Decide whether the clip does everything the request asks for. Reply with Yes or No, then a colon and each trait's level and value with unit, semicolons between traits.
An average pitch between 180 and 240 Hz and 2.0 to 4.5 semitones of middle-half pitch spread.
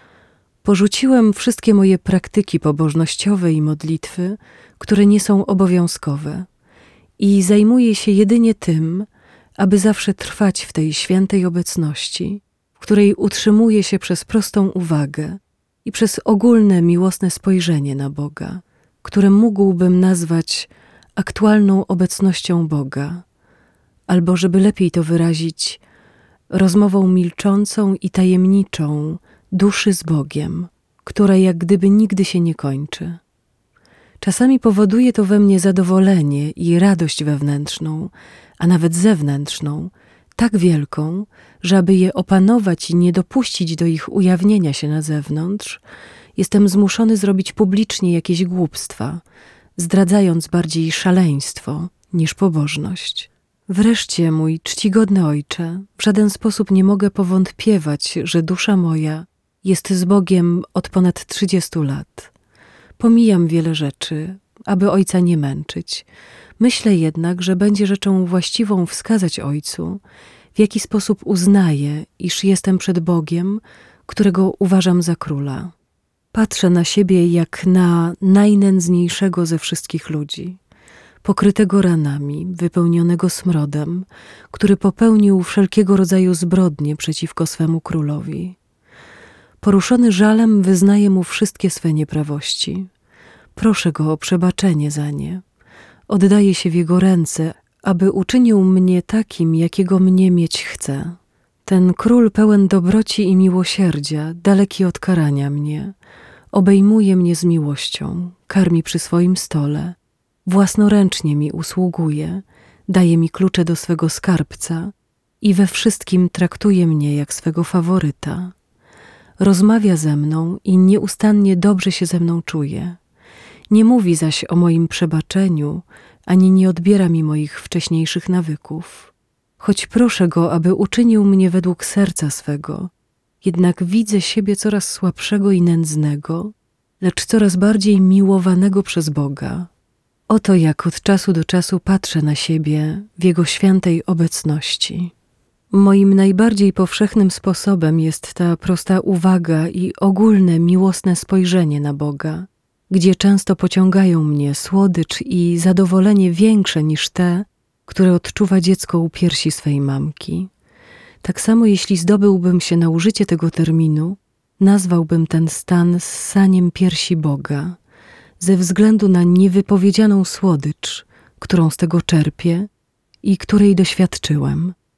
Yes: medium, 185 Hz; average, 3.1 semitones